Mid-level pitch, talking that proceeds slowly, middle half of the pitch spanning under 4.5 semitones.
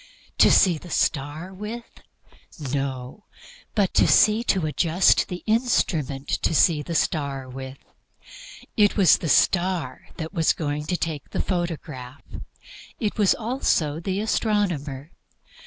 No: medium, 165 Hz; slow, 125 wpm; average, 5.3 semitones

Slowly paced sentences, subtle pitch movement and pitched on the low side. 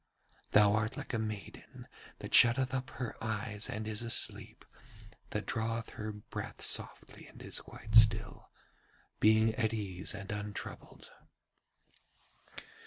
Yes: slow, 125 wpm; narrow, 1.4 semitones; low, 110 Hz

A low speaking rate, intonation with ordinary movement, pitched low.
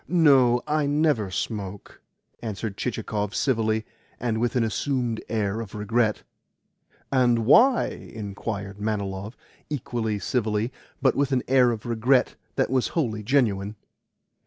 Yes: slow, 115 wpm; average, 3.7 semitones; low, 115 Hz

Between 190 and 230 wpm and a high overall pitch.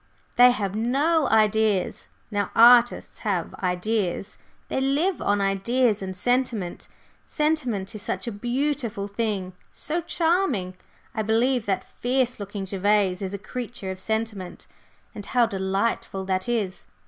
No: slow, 135 wpm; high, 215 Hz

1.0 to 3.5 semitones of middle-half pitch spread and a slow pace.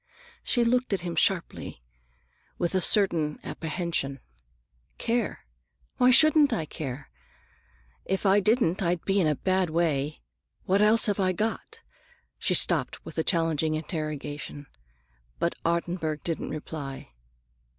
No: average, 4.4 semitones; slow, 130 wpm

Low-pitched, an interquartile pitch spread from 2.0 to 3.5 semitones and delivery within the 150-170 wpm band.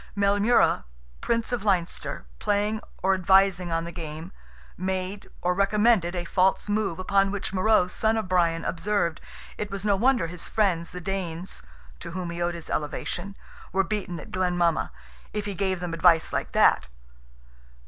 No: medium, 185 Hz; average, 2.8 semitones; average, 165 wpm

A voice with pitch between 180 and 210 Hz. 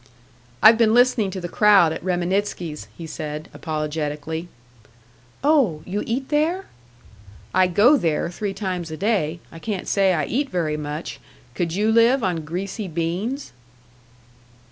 Yes: medium, 185 Hz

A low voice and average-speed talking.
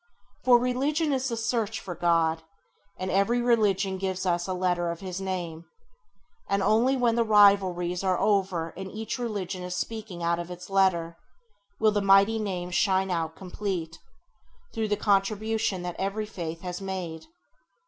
No: high, 190 Hz; average, 160 wpm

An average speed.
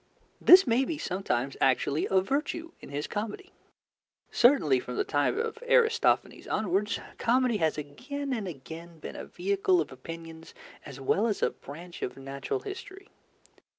Yes: average, 150 wpm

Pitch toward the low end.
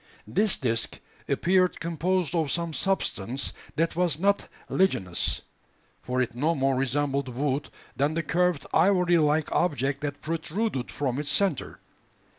No: medium, 155 Hz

